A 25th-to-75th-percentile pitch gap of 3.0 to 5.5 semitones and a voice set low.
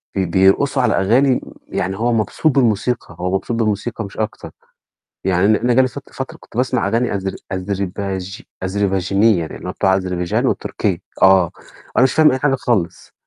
Yes: average, 4.2 semitones; low, 100 Hz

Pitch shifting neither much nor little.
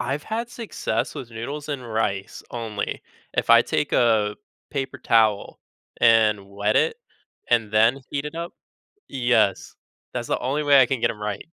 Yes: average, 4.6 semitones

